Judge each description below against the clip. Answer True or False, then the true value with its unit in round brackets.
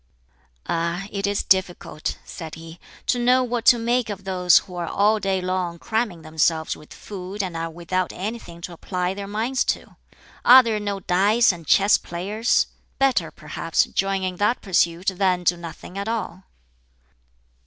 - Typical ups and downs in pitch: True (3.4 semitones)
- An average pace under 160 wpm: False (165 wpm)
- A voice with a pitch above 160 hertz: True (190 Hz)